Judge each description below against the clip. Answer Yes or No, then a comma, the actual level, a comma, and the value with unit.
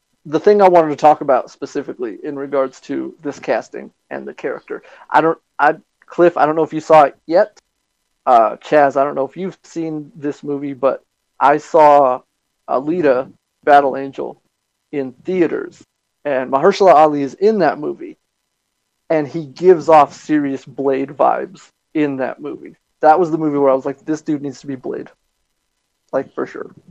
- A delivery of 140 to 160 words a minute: No, average, 180 wpm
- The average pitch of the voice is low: No, medium, 145 Hz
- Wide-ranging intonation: No, average, 3.0 semitones